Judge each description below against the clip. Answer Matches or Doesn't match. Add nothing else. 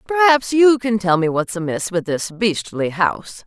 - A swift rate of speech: Doesn't match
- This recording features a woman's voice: Matches